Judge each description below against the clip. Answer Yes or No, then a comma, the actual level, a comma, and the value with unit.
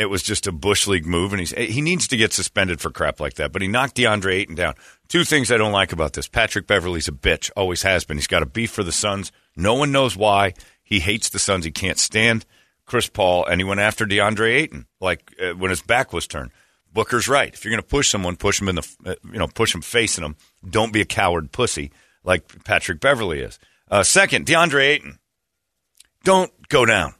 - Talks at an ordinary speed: No, fast, 235 wpm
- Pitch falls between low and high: No, low, 100 Hz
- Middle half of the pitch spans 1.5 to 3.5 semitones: No, average, 4.2 semitones